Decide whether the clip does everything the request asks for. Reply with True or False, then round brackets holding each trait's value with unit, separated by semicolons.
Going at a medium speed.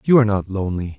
False (245 wpm)